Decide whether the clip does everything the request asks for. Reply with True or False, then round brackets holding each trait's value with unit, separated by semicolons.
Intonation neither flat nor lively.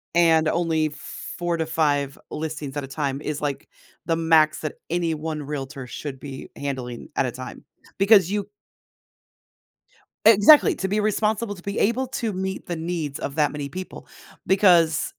True (4.6 semitones)